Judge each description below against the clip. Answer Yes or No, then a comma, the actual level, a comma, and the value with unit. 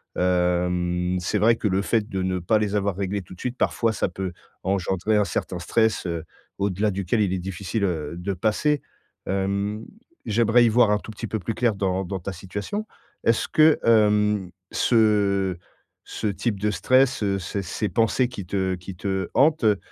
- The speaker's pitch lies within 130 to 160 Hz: No, low, 100 Hz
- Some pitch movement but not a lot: Yes, average, 3.0 semitones